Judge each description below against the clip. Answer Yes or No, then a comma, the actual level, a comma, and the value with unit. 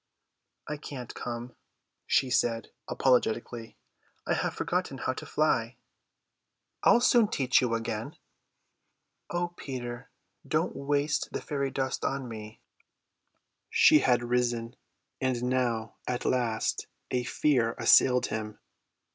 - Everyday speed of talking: No, slow, 115 wpm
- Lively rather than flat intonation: No, narrow, 2.5 semitones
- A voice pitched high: No, low, 125 Hz